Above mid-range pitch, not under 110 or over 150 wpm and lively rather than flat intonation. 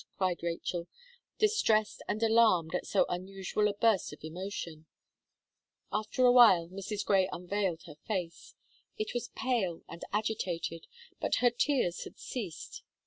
No: high, 195 Hz; average, 140 wpm; average, 4.5 semitones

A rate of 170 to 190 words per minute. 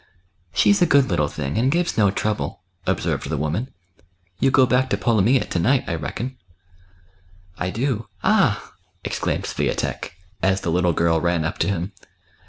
Yes: average, 185 wpm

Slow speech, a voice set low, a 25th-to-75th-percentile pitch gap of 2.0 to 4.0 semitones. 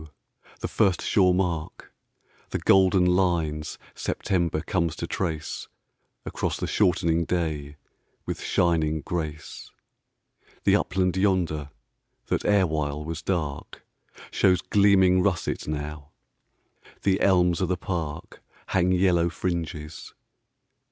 Yes: slow, 90 wpm; very low, 85 Hz; average, 3.1 semitones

